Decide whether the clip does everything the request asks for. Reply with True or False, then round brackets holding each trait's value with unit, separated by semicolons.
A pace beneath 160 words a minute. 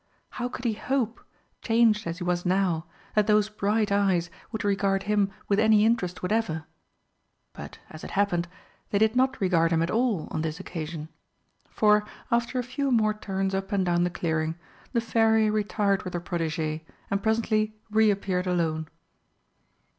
False (170 wpm)